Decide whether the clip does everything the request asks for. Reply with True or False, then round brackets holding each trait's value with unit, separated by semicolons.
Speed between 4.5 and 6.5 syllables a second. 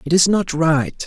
False (4.1 syllables/s)